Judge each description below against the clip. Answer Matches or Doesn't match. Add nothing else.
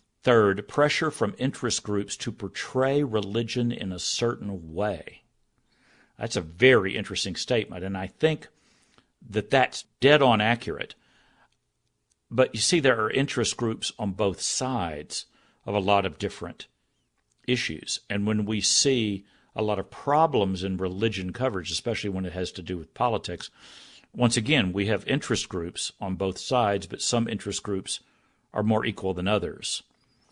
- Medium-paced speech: Matches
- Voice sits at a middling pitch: Doesn't match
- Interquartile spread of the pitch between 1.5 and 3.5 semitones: Doesn't match